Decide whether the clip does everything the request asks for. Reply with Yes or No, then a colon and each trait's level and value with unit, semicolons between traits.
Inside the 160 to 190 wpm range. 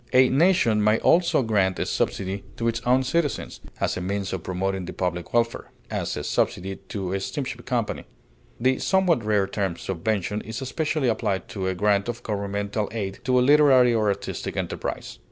Yes: average, 180 wpm